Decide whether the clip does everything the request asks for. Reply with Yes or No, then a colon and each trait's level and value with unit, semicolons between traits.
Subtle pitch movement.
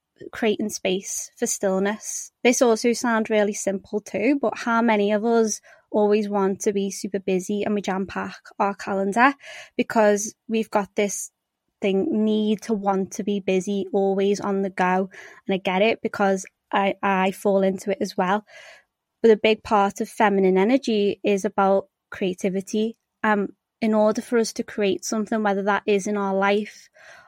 Yes: narrow, 2.2 semitones